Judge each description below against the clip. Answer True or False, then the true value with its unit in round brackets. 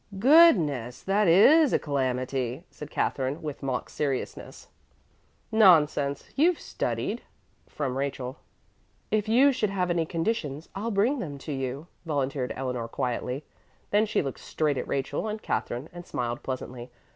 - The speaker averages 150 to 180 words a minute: False (140 wpm)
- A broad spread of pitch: True (7.3 semitones)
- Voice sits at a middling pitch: True (150 Hz)